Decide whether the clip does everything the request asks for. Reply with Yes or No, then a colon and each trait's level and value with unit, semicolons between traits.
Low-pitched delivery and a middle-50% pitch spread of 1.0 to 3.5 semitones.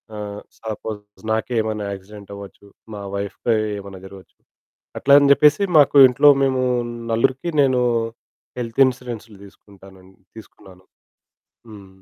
No: low, 105 Hz; average, 4.0 semitones